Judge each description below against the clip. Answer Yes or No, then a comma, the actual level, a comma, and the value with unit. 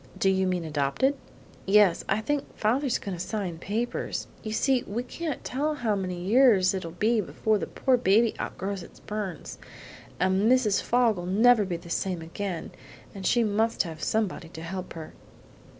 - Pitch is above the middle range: Yes, high, 200 Hz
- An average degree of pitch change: Yes, average, 4.2 semitones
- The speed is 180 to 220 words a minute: No, average, 170 wpm